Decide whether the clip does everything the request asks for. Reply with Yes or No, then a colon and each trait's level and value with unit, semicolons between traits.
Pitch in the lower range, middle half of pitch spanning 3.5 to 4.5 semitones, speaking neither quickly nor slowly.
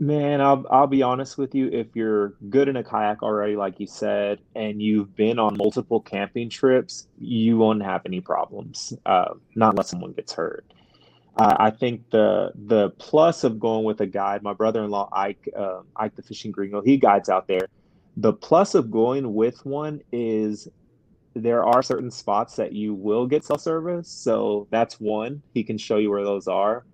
Yes: low, 110 Hz; average, 3.8 semitones; average, 190 wpm